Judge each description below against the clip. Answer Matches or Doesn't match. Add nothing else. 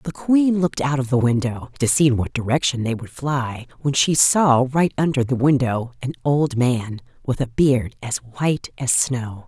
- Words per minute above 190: Matches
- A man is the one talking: Doesn't match